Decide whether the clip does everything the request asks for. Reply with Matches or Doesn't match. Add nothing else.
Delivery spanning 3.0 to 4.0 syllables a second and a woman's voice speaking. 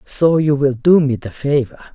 Doesn't match